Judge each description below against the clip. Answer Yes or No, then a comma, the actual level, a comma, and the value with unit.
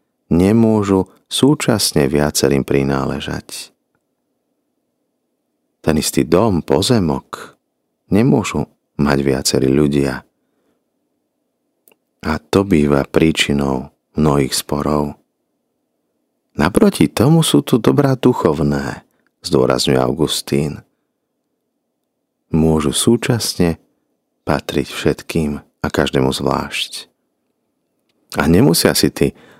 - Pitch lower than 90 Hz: Yes, very low, 75 Hz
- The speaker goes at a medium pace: No, slow, 75 wpm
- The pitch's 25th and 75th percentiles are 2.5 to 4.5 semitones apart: No, wide, 5.4 semitones